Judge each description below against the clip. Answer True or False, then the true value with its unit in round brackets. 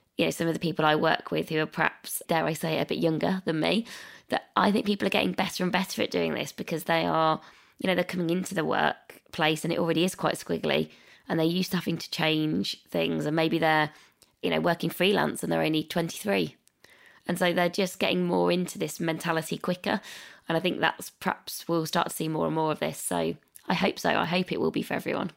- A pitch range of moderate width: False (2.3 semitones)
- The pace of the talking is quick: True (240 wpm)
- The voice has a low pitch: False (165 Hz)